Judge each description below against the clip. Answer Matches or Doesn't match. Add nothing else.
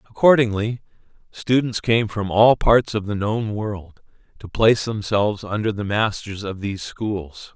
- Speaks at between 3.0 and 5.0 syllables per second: Matches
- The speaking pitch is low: Matches